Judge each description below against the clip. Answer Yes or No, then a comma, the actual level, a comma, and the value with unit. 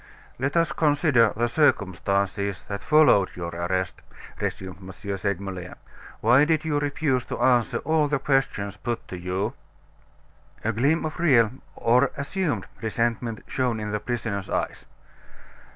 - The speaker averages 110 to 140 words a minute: Yes, slow, 135 wpm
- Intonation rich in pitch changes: Yes, wide, 6.2 semitones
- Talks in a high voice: No, low, 115 Hz